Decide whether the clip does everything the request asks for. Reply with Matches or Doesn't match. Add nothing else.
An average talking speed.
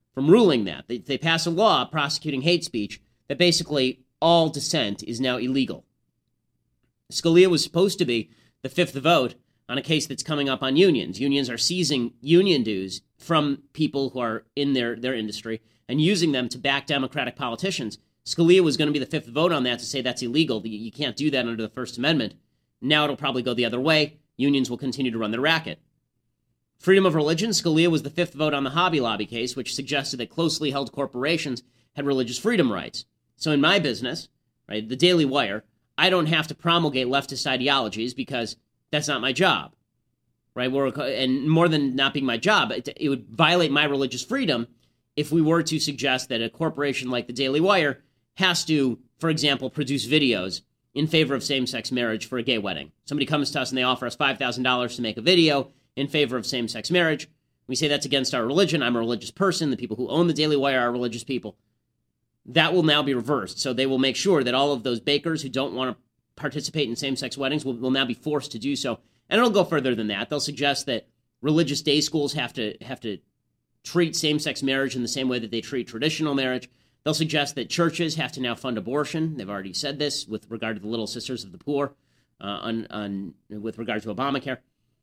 Doesn't match